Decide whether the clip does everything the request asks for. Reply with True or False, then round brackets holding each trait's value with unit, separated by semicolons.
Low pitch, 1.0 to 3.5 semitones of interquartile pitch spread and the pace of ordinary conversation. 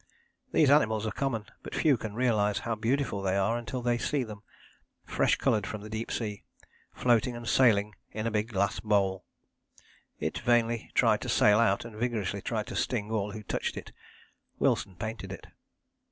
True (110 Hz; 2.4 semitones; 180 wpm)